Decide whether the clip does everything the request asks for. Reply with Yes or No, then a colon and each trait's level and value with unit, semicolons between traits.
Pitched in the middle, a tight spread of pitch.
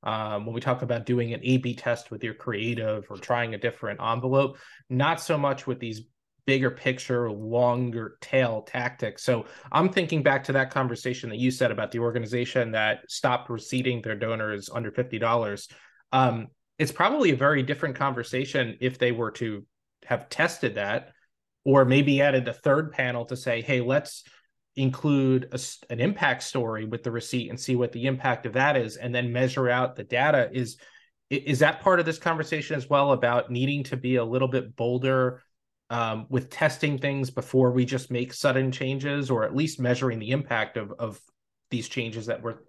No: low, 125 Hz; narrow, 2.3 semitones